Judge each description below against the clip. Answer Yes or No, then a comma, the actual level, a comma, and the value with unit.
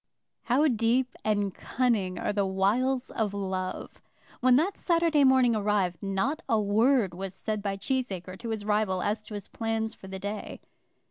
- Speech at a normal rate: Yes, average, 170 wpm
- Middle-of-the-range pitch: No, high, 215 Hz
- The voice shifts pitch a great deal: No, average, 4.2 semitones